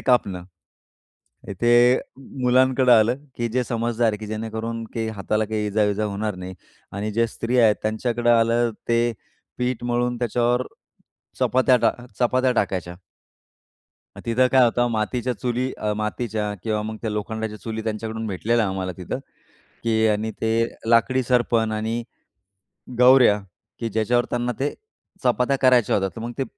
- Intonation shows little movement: Yes, narrow, 2.2 semitones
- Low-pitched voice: Yes, low, 115 Hz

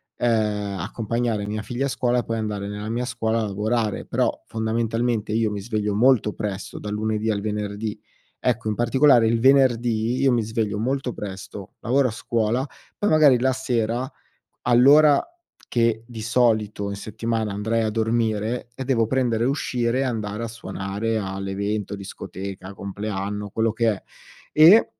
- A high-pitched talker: No, low, 110 Hz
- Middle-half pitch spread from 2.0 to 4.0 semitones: Yes, narrow, 2.5 semitones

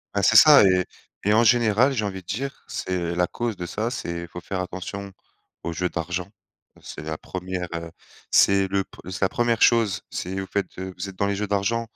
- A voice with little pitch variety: No, average, 3.2 semitones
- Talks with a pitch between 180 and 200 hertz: No, very low, 95 Hz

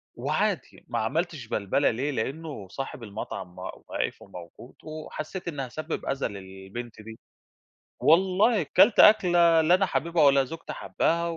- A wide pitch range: Yes, wide, 7.2 semitones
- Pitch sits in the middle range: Yes, medium, 145 Hz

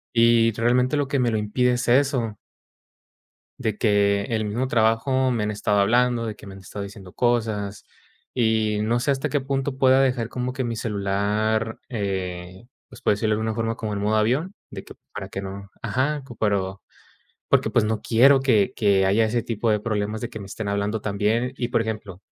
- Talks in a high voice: No, low, 110 Hz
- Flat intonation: No, average, 3.1 semitones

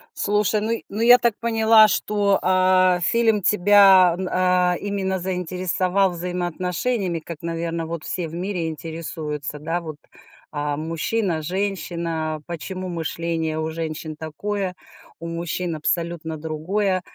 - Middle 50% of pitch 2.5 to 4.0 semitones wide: Yes, average, 3.2 semitones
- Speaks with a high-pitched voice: No, medium, 180 Hz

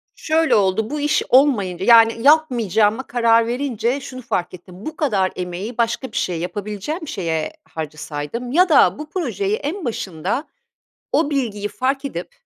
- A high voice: Yes, high, 230 Hz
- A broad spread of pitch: Yes, wide, 6.9 semitones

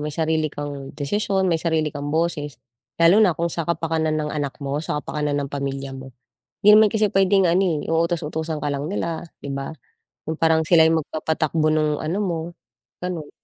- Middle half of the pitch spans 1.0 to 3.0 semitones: Yes, narrow, 2.5 semitones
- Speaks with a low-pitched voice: No, medium, 160 Hz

